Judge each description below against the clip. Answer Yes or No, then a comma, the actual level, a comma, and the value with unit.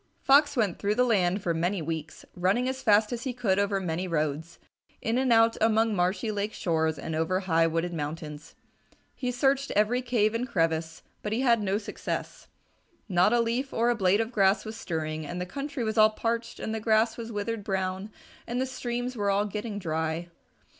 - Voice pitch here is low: No, high, 210 Hz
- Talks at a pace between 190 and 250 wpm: Yes, average, 200 wpm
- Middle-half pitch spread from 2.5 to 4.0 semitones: No, average, 4.8 semitones